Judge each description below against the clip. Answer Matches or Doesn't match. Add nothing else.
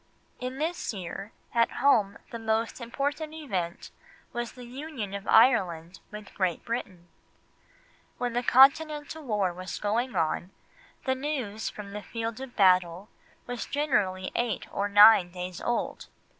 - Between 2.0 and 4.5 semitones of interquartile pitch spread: Doesn't match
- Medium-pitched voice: Doesn't match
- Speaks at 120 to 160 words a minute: Matches